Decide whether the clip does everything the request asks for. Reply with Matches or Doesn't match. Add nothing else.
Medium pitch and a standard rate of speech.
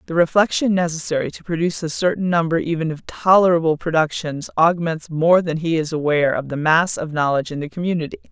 Matches